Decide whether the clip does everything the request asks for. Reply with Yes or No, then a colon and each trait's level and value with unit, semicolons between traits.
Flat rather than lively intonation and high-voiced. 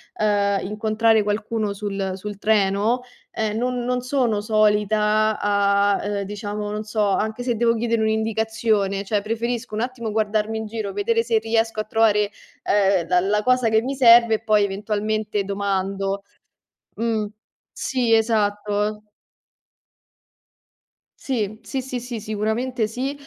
Yes: narrow, 1.8 semitones; high, 215 Hz